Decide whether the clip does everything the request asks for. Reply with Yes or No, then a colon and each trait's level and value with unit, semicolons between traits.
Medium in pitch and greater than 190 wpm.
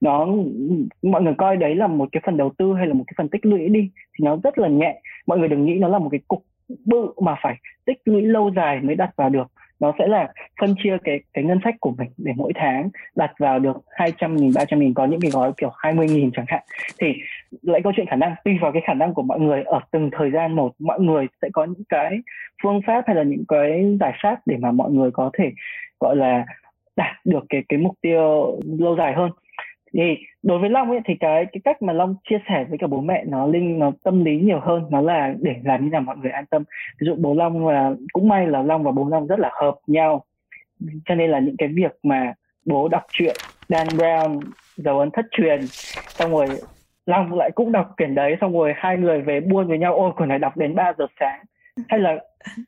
Yes: medium, 165 Hz; average, 245 wpm